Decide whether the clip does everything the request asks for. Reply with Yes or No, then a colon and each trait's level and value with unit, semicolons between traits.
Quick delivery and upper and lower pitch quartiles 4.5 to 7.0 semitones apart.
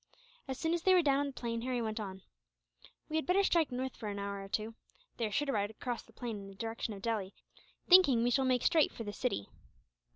Yes: fast, 255 wpm; average, 4.8 semitones